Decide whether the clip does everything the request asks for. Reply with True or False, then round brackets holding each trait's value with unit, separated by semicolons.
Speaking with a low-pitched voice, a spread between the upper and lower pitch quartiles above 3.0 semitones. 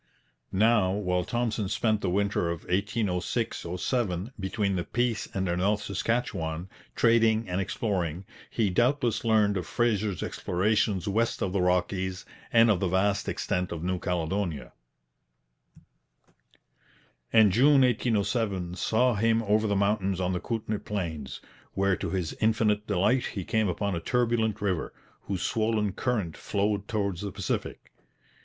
True (100 Hz; 3.4 semitones)